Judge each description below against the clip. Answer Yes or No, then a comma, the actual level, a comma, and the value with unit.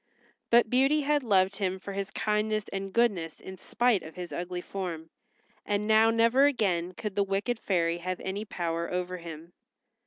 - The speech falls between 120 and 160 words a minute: No, average, 175 wpm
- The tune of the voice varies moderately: Yes, average, 3.6 semitones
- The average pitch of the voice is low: No, high, 195 Hz